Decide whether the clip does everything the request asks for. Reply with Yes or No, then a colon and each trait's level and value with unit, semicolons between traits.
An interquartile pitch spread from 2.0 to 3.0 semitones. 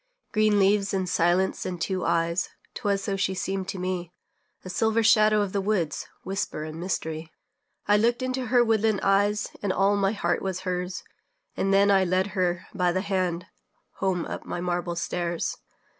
Yes: narrow, 2.4 semitones